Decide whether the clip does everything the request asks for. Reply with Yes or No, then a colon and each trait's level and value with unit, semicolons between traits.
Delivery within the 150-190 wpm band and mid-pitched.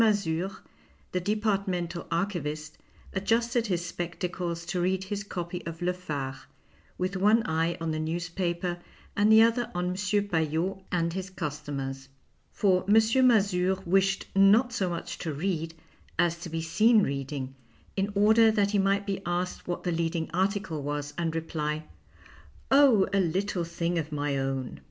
Yes: average, 155 wpm; medium, 180 Hz